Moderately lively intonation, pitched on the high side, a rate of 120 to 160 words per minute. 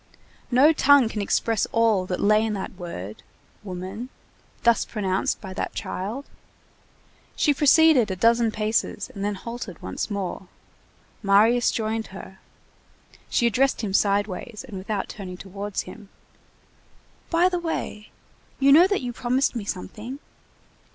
Yes: average, 3.9 semitones; high, 215 Hz; average, 140 wpm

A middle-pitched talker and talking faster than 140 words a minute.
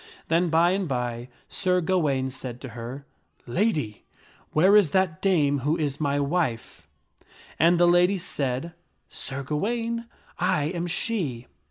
Yes: medium, 160 Hz; average, 160 wpm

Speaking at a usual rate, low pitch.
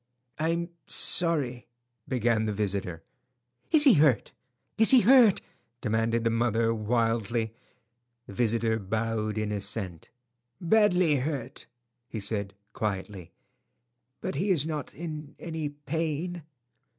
No: slow, 100 wpm; low, 115 Hz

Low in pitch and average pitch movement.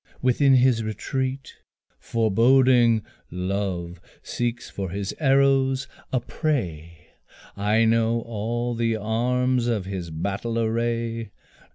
Yes: low, 115 Hz; average, 3.8 semitones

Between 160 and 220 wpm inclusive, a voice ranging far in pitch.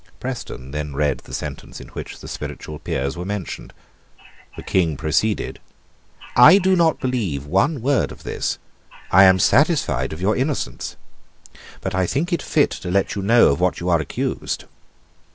Yes: average, 170 wpm; wide, 8.7 semitones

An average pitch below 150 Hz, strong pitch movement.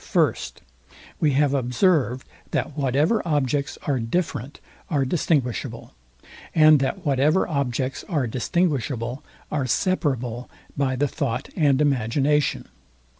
No: medium, 140 Hz; average, 3.0 semitones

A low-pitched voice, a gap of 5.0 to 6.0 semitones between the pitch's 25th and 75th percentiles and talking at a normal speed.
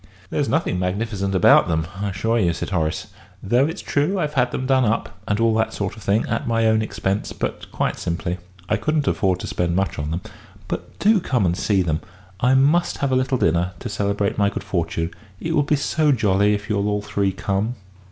No: low, 105 Hz; wide, 5.4 semitones; fast, 220 wpm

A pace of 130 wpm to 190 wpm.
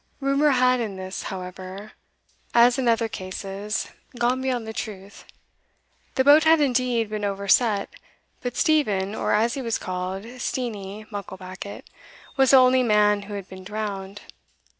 Yes: average, 145 wpm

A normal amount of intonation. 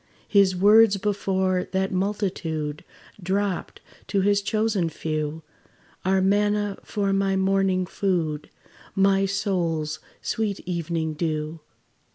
Yes: average, 3.0 semitones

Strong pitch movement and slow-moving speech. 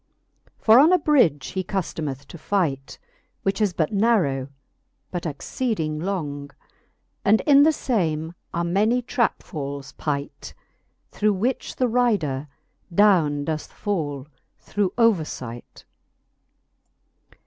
Yes: wide, 7.0 semitones; slow, 115 wpm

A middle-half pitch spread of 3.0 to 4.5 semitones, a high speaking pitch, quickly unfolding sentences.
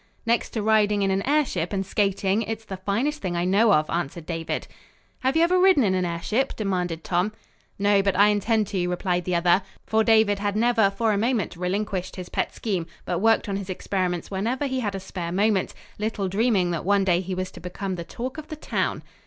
Yes: average, 3.5 semitones; high, 200 Hz; fast, 220 wpm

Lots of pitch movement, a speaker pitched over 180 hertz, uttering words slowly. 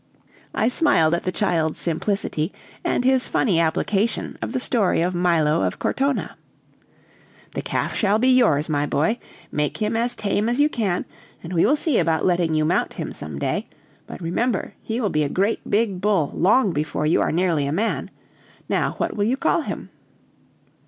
No: wide, 6.0 semitones; high, 190 Hz; average, 180 wpm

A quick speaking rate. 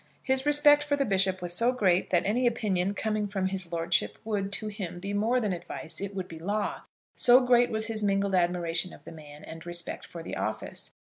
Yes: fast, 215 wpm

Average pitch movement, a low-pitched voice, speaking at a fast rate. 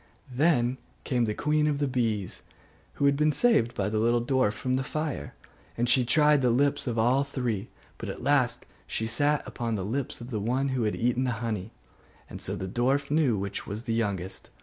Yes: average, 3.9 semitones; low, 125 Hz; fast, 210 wpm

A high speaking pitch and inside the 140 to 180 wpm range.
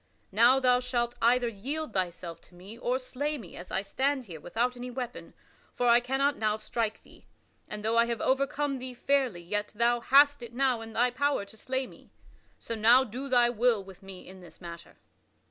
No: high, 240 Hz; average, 200 wpm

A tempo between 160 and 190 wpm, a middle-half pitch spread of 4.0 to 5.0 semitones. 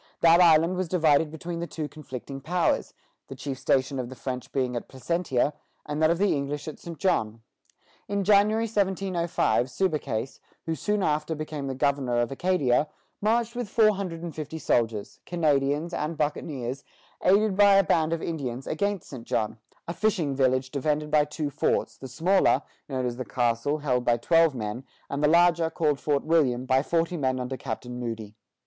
Yes: average, 180 wpm; average, 4.7 semitones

